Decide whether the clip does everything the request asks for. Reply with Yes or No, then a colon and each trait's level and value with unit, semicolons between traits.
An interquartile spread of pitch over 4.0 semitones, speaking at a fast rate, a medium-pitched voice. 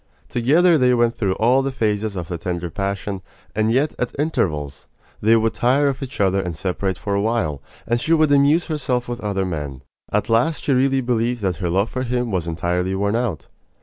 No: average, 5.2 semitones; fast, 210 wpm; low, 110 Hz